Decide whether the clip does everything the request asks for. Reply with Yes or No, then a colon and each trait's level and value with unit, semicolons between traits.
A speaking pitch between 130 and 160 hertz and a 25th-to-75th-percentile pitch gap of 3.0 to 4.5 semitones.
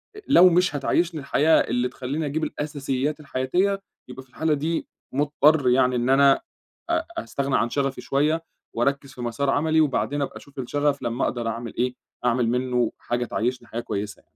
Yes: low, 135 Hz; average, 3.4 semitones